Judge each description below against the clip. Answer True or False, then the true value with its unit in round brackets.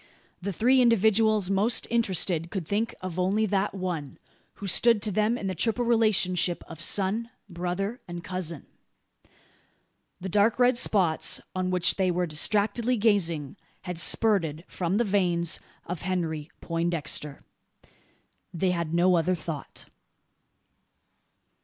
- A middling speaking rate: False (130 wpm)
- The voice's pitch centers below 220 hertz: True (185 Hz)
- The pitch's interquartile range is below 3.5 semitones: False (3.8 semitones)